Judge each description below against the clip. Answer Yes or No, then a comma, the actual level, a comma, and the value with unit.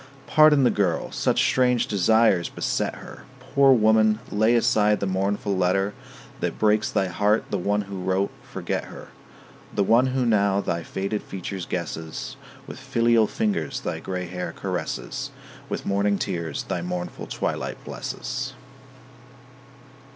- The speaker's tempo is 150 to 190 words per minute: No, average, 140 wpm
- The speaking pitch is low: Yes, low, 100 Hz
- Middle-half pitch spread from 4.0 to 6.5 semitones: No, average, 3.6 semitones